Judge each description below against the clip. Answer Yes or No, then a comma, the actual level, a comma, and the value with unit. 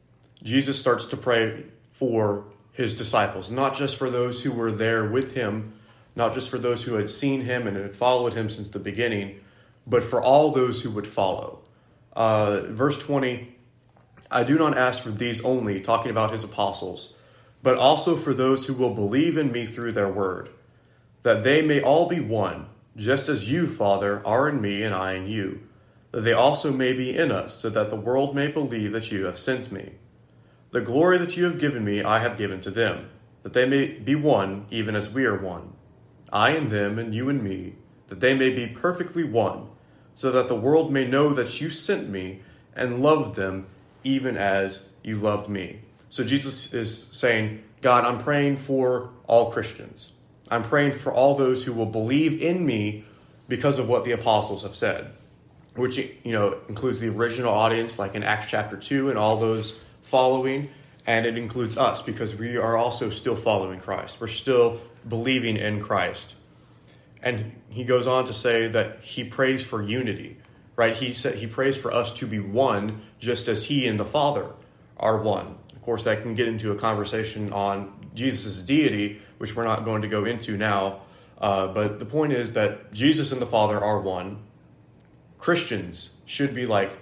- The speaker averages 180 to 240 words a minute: Yes, average, 190 wpm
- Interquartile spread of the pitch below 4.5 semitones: Yes, average, 3.8 semitones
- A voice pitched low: Yes, low, 115 Hz